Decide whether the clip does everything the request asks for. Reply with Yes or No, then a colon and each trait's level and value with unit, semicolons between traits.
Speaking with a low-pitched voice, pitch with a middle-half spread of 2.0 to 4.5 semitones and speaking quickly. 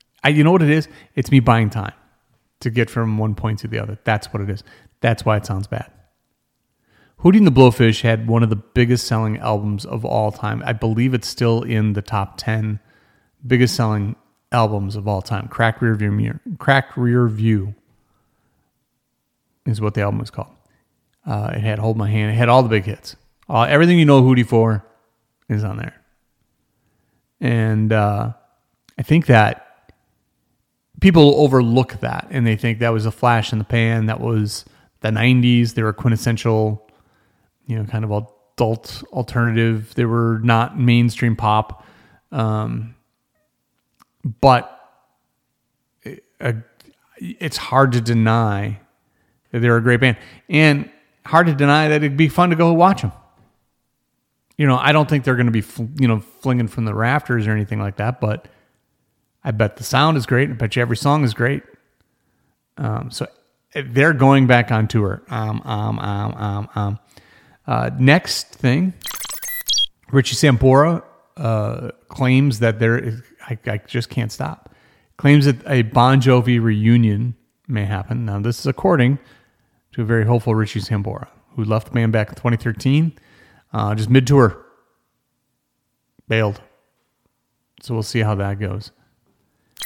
No: low, 115 Hz; average, 3.0 semitones; average, 160 wpm